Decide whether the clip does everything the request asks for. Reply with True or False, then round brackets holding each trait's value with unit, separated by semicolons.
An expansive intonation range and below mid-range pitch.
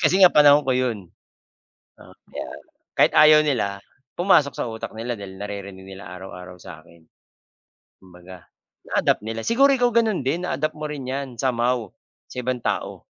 True (7.6 semitones; 125 Hz)